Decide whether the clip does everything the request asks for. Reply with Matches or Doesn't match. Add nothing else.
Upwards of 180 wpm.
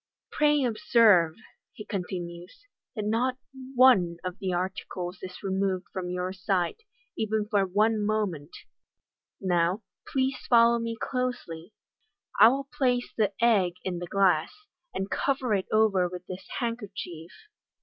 Doesn't match